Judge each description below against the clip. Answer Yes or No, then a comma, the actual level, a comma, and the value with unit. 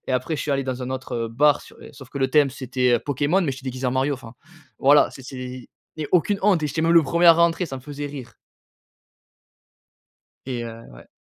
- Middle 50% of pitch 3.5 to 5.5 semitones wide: No, average, 3.0 semitones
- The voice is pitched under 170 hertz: Yes, low, 135 Hz